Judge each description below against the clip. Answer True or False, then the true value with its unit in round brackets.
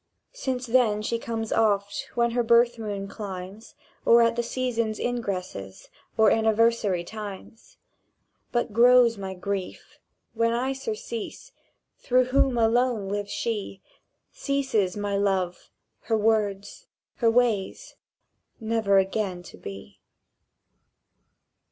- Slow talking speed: True (115 wpm)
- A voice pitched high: True (220 Hz)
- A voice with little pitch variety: False (3.0 semitones)